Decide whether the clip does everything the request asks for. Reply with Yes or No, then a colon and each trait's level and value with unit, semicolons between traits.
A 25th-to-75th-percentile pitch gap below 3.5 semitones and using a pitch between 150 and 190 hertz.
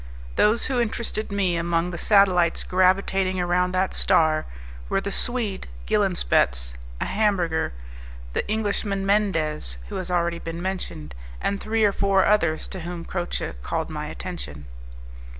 Yes: average, 3.1 semitones; medium, 185 Hz